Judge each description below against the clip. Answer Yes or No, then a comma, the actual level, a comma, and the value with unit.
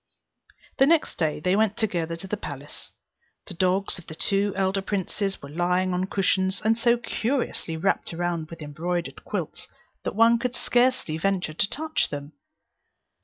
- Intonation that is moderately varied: Yes, average, 4.4 semitones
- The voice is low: No, high, 190 Hz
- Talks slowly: No, average, 165 wpm